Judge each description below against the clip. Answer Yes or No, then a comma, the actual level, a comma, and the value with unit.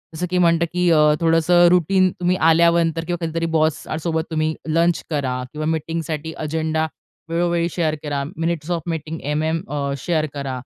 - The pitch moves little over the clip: Yes, narrow, 1.6 semitones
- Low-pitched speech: No, medium, 160 Hz